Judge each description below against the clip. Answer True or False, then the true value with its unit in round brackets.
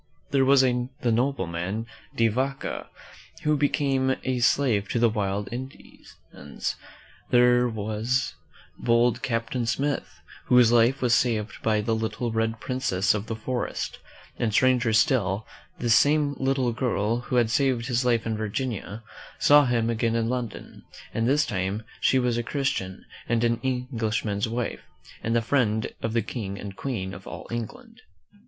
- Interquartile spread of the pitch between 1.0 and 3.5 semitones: True (2.8 semitones)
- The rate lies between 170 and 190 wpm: False (155 wpm)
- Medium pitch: False (115 Hz)